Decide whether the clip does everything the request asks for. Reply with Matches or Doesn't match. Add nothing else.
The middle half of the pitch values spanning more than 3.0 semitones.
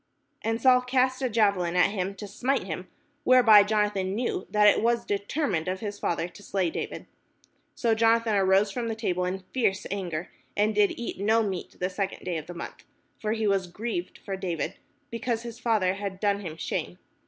Matches